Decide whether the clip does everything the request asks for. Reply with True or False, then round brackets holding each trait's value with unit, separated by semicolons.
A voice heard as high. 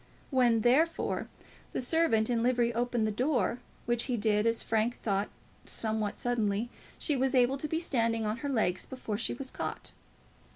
True (240 Hz)